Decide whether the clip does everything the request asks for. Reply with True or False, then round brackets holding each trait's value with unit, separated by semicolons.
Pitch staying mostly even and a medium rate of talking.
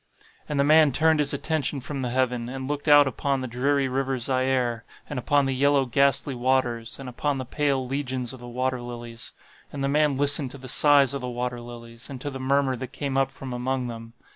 False (2.2 semitones; 220 wpm)